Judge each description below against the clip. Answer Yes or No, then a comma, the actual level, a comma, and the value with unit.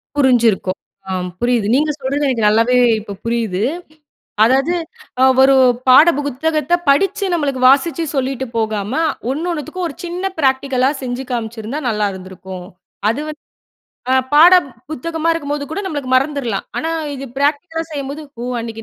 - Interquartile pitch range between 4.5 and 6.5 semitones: Yes, average, 4.8 semitones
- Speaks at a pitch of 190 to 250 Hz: No, very high, 270 Hz